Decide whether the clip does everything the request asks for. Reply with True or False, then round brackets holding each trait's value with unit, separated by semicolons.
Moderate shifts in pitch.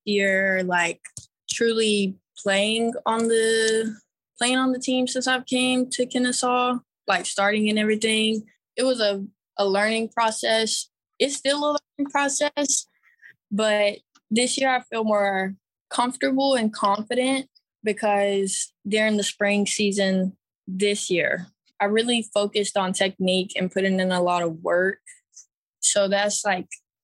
True (3.9 semitones)